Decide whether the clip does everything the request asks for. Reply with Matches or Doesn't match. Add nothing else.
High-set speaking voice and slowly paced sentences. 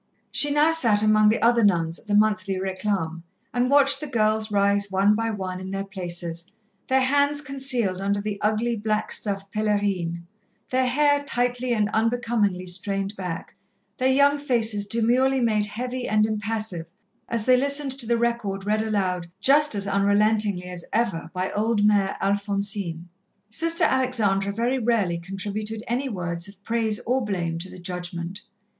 Doesn't match